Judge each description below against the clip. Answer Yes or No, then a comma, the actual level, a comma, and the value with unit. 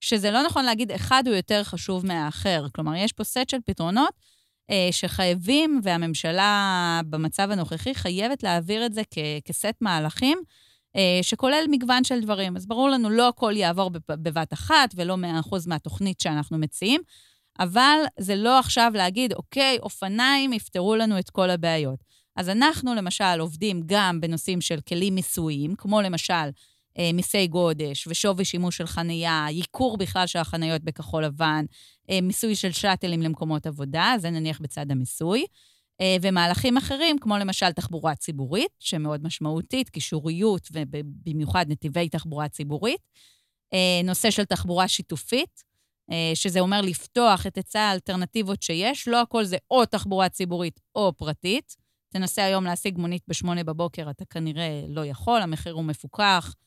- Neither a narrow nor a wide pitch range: Yes, average, 4.8 semitones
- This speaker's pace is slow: No, average, 140 wpm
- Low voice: No, medium, 185 Hz